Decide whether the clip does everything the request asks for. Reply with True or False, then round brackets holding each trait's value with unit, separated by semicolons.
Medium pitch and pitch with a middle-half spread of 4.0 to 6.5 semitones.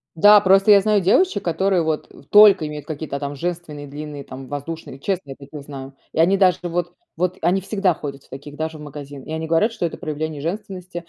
True (160 Hz; 4.5 semitones)